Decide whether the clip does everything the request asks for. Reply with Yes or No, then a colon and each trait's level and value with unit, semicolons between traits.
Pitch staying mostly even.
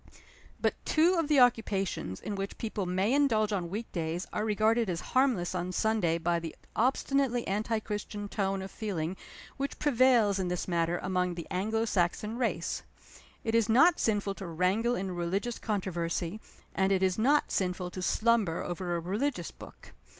No: average, 4.2 semitones